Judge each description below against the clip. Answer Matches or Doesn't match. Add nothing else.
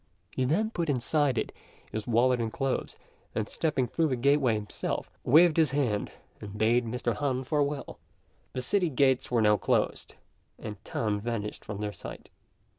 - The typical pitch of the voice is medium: Doesn't match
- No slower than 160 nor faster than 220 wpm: Matches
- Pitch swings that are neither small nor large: Matches